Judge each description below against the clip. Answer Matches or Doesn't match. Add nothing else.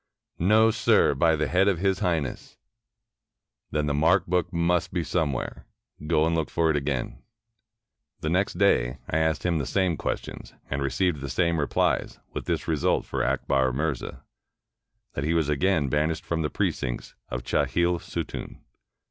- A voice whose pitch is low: Matches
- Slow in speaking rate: Doesn't match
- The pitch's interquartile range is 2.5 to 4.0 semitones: Matches